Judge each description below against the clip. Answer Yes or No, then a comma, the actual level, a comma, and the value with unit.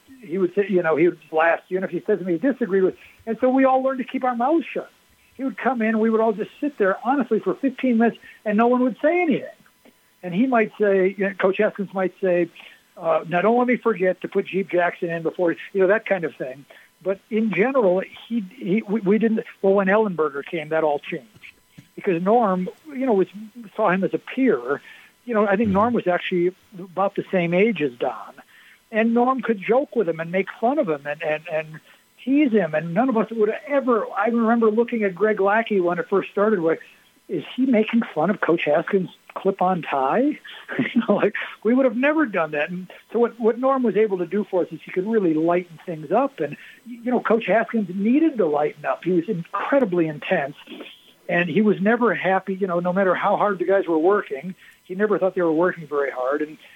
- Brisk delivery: Yes, fast, 235 wpm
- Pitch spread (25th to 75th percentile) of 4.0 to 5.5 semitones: Yes, average, 4.6 semitones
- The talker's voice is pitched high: Yes, high, 200 Hz